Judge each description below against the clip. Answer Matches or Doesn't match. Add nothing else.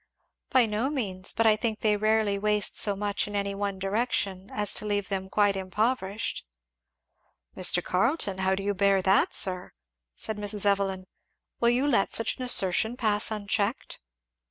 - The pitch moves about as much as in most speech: Doesn't match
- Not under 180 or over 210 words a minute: Doesn't match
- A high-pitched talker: Matches